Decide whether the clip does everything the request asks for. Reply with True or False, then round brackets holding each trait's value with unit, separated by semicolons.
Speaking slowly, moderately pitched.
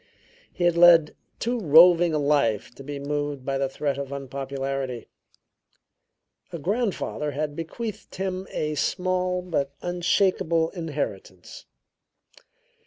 True (110 wpm; 155 Hz)